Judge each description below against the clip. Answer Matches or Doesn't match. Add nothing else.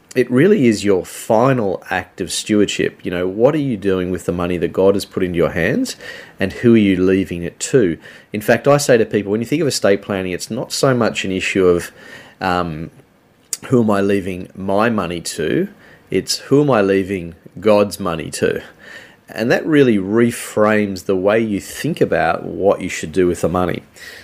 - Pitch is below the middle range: Matches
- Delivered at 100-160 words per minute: Doesn't match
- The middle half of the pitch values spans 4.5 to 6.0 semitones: Doesn't match